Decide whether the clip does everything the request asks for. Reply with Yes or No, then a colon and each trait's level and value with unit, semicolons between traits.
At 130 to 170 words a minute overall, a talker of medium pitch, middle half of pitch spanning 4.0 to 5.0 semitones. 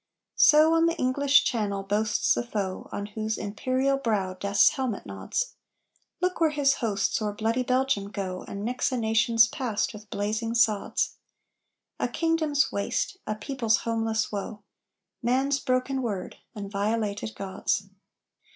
No: average, 140 wpm; high, 225 Hz; average, 4.5 semitones